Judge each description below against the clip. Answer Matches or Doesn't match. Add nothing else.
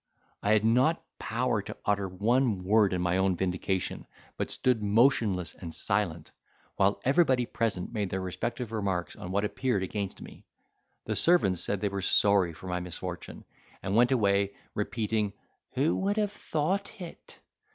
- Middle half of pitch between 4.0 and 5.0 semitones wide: Matches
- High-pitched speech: Doesn't match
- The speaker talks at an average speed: Matches